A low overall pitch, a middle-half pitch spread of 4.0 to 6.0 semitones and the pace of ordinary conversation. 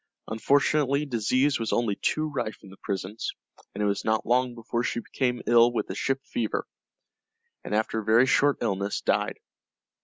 No: low, 120 Hz; average, 3.6 semitones; average, 175 wpm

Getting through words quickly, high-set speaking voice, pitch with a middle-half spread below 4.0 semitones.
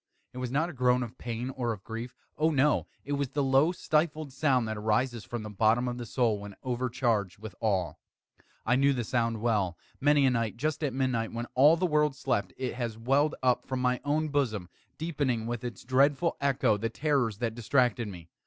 No: fast, 210 wpm; low, 125 Hz; average, 3.6 semitones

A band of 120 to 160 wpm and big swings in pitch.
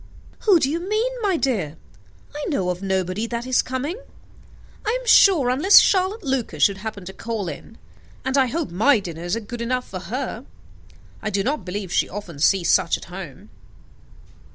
No: average, 180 wpm; wide, 7.2 semitones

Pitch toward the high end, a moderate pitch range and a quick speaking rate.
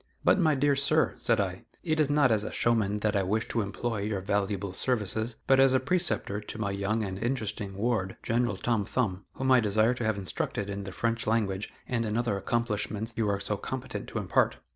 No: low, 110 Hz; average, 3.4 semitones; fast, 215 wpm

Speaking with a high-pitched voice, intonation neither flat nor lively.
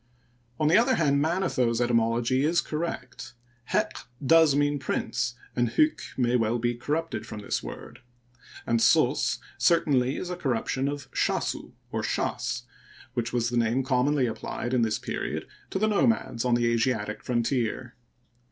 No: low, 125 Hz; average, 3.8 semitones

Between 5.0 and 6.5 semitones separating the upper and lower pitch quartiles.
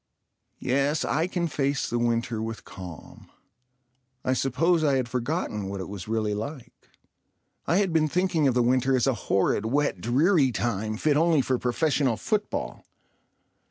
Yes: wide, 5.4 semitones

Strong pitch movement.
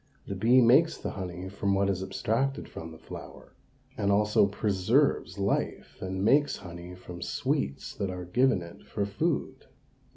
No: average, 3.9 semitones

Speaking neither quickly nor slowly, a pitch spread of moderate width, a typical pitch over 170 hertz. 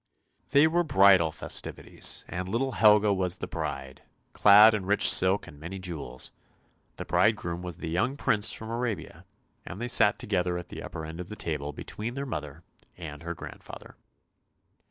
No: average, 170 wpm; average, 4.5 semitones; very low, 95 Hz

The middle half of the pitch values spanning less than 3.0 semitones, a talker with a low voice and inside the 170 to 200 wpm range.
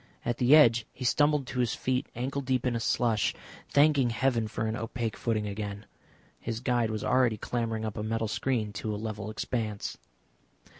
Yes: narrow, 2.6 semitones; low, 115 Hz; average, 180 wpm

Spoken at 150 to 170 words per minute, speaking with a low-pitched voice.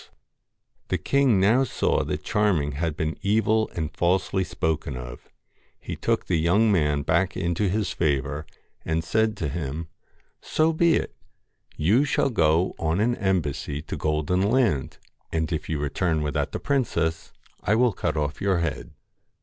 Yes: average, 165 wpm; very low, 85 Hz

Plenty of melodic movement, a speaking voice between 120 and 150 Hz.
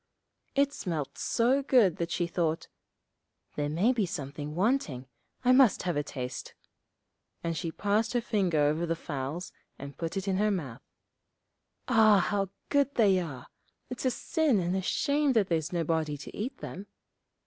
No: wide, 6.2 semitones; medium, 185 Hz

